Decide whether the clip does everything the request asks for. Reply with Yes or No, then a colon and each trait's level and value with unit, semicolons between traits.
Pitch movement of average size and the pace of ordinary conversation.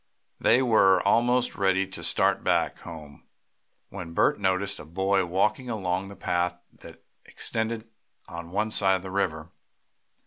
Yes: average, 3.1 semitones; average, 145 wpm